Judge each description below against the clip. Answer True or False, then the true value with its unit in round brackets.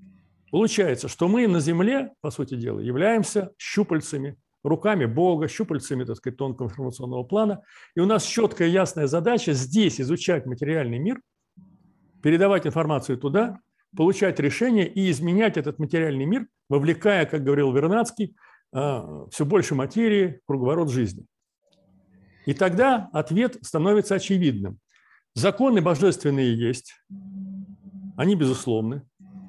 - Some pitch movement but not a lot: False (6.7 semitones)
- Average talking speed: True (120 wpm)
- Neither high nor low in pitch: True (165 Hz)